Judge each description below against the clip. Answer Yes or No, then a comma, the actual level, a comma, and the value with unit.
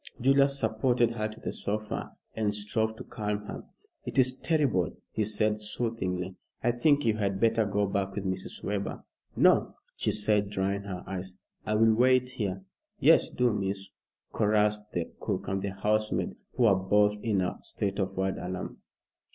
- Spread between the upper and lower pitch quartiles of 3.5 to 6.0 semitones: No, narrow, 2.5 semitones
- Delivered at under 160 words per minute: No, average, 170 wpm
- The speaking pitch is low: Yes, low, 105 Hz